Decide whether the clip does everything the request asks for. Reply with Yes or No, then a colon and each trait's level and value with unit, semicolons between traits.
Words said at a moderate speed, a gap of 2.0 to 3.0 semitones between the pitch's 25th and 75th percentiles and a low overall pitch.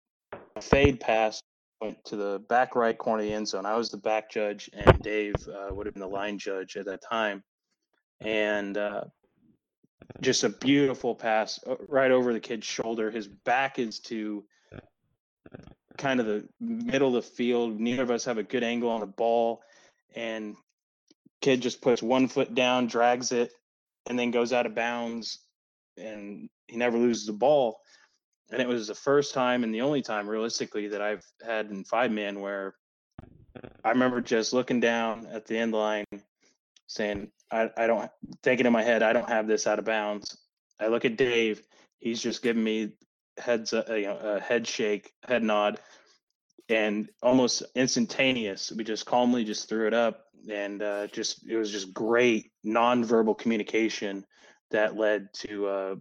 Yes: average, 175 wpm; narrow, 2.4 semitones; low, 115 Hz